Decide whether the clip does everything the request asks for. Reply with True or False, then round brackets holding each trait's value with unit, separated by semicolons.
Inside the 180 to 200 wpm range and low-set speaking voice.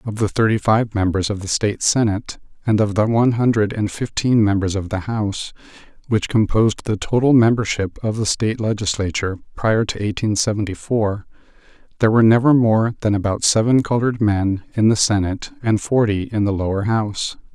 False (170 wpm; 110 Hz)